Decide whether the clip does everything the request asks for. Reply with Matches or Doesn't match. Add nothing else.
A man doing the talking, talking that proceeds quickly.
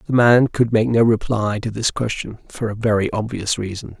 Matches